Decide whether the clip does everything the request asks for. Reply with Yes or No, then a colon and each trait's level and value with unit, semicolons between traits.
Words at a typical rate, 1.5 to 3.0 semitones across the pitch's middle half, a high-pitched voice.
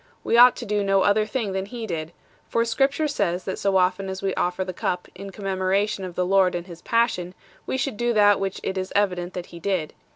No: fast, 235 wpm; narrow, 2.6 semitones; high, 195 Hz